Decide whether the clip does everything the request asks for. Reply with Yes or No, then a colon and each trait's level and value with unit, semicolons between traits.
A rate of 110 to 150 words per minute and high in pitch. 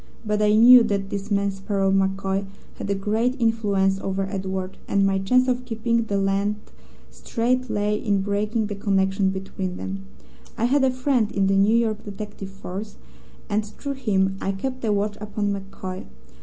No: average, 175 wpm; high, 205 Hz